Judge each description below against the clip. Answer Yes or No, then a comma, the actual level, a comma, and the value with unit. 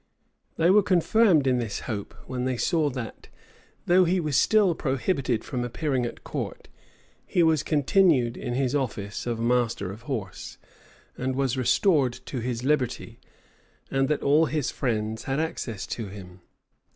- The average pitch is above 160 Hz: No, low, 130 Hz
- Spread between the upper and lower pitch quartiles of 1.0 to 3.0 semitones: No, average, 4.8 semitones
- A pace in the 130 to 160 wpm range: Yes, average, 155 wpm